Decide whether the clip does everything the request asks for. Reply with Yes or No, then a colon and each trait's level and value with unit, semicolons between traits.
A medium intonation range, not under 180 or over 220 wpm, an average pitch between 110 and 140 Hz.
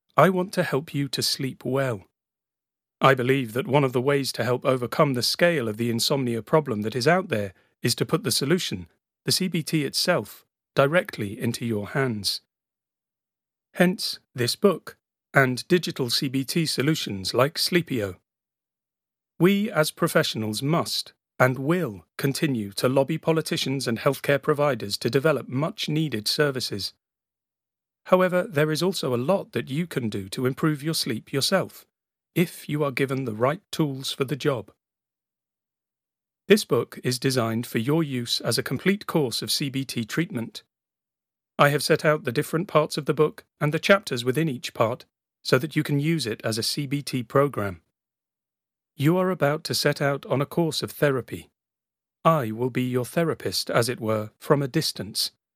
No: average, 5.0 semitones; average, 165 wpm; low, 135 Hz